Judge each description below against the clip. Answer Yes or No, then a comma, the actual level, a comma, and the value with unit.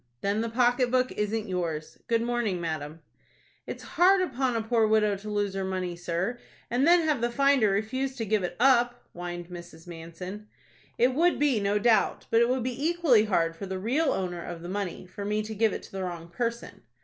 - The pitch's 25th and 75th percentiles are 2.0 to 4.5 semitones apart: No, average, 5.1 semitones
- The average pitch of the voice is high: Yes, high, 215 Hz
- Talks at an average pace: No, fast, 210 wpm